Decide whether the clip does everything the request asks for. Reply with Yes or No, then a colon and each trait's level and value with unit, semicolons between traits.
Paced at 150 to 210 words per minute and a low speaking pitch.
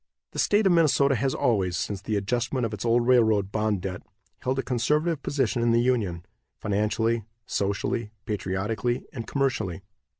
Yes: average, 160 wpm; low, 115 Hz